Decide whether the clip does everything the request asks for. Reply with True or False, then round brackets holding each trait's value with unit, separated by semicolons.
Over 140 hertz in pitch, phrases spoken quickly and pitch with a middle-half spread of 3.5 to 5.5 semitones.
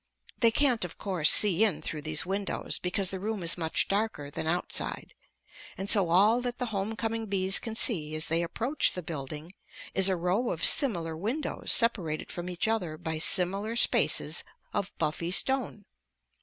False (190 Hz; 175 wpm; 5.0 semitones)